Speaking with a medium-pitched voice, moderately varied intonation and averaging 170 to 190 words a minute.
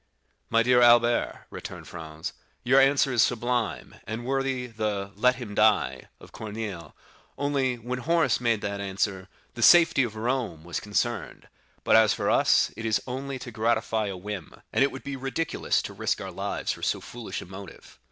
No: low, 115 Hz; average, 3.7 semitones; average, 180 wpm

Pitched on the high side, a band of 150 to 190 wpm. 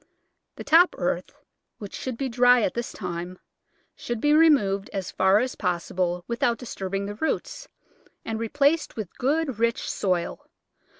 Yes: high, 225 Hz; average, 165 wpm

